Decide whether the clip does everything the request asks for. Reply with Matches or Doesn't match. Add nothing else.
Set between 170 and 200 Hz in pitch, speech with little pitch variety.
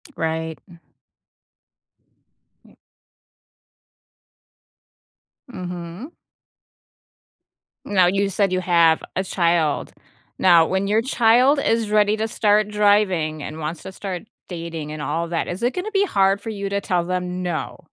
Doesn't match